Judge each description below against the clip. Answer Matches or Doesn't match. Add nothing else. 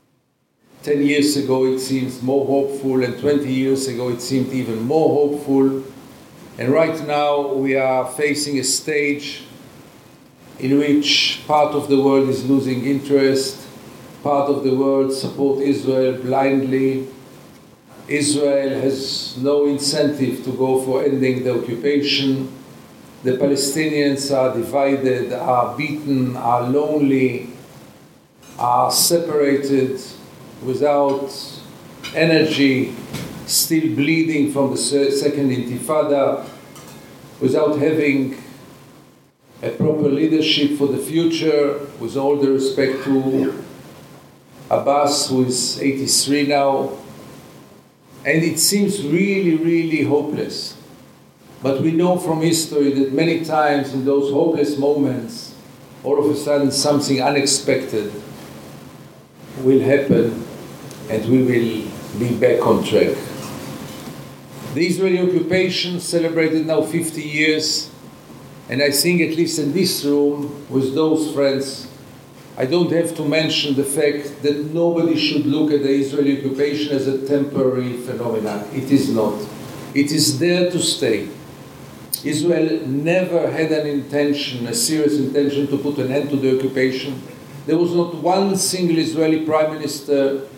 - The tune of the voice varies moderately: Doesn't match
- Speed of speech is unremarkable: Doesn't match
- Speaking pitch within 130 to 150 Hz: Matches